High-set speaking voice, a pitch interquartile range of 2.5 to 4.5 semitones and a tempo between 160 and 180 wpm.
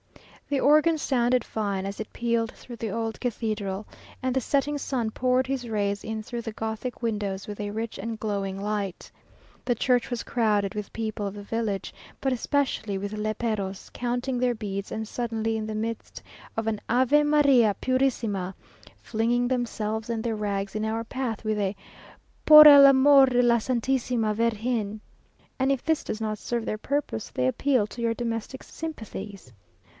Yes: high, 225 Hz; average, 3.1 semitones; average, 170 wpm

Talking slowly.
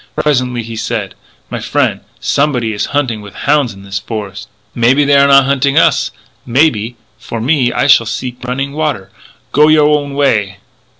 No: average, 180 wpm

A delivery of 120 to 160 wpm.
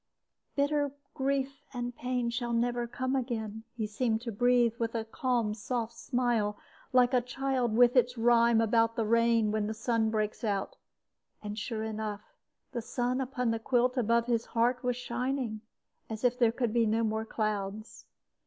No: average, 170 wpm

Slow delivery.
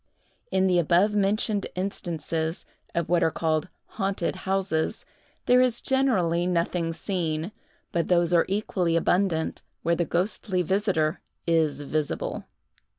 Yes: slow, 120 wpm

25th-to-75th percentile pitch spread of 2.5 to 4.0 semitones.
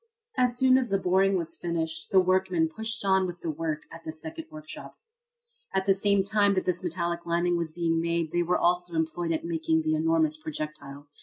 Yes: average, 3.0 semitones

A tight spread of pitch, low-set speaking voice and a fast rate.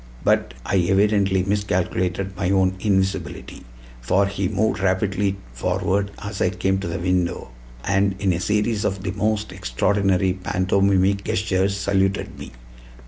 No: narrow, 1.3 semitones; very low, 95 Hz; average, 140 wpm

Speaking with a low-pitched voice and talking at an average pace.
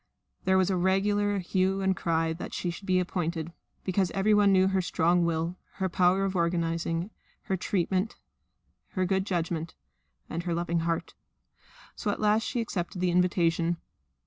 No: medium, 180 Hz; average, 165 wpm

